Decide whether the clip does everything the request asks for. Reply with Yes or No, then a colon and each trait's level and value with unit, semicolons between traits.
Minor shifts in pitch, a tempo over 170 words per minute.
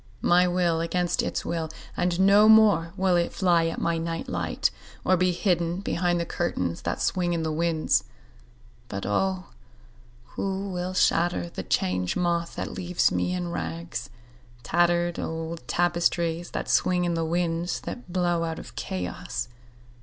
No: narrow, 1.6 semitones; average, 150 wpm